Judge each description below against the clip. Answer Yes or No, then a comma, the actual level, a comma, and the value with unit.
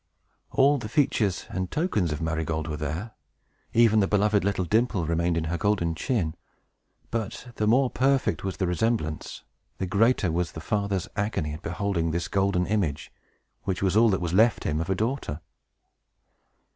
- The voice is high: No, very low, 95 Hz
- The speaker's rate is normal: Yes, average, 170 wpm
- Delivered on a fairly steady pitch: No, average, 4.7 semitones